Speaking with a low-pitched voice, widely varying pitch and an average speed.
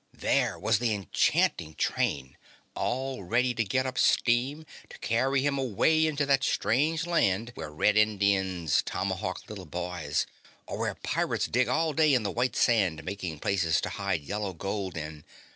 Yes: low, 105 Hz; wide, 6.1 semitones; average, 160 wpm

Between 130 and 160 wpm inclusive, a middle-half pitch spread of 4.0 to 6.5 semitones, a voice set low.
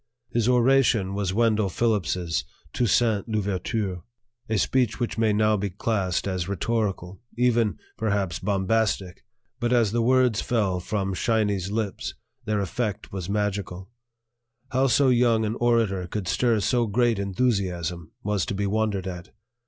No: average, 140 wpm; average, 3.3 semitones; low, 105 Hz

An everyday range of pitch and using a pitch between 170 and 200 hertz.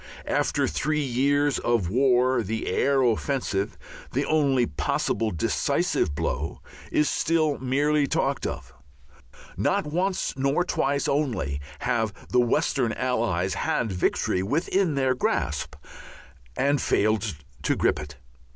No: average, 4.8 semitones; low, 130 Hz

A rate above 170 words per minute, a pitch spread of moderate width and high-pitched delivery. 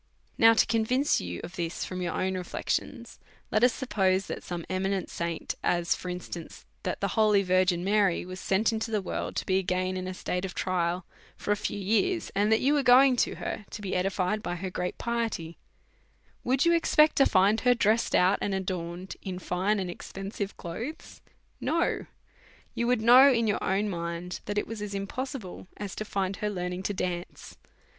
Yes: average, 195 wpm; average, 3.5 semitones; high, 195 Hz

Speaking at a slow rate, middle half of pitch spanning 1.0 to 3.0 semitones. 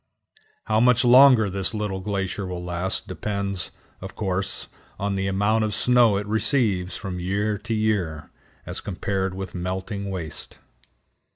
No: average, 145 wpm; narrow, 2.5 semitones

